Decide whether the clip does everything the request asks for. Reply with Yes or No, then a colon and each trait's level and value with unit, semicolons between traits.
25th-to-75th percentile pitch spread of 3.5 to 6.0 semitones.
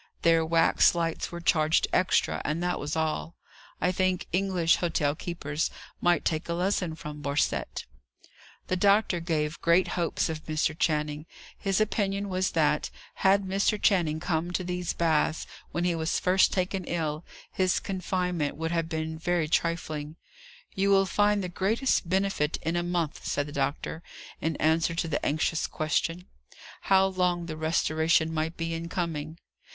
No: narrow, 2.5 semitones